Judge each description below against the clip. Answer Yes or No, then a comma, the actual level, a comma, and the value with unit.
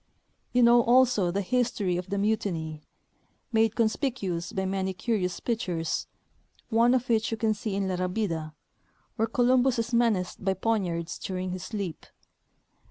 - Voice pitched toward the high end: Yes, high, 205 Hz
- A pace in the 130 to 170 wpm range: Yes, average, 155 wpm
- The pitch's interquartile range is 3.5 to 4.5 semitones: Yes, average, 4.2 semitones